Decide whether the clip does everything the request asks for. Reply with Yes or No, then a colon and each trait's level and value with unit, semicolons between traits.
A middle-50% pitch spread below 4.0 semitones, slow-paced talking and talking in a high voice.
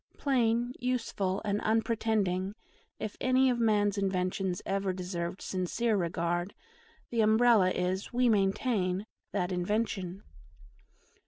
Yes: average, 3.6 semitones; slow, 105 wpm; high, 200 Hz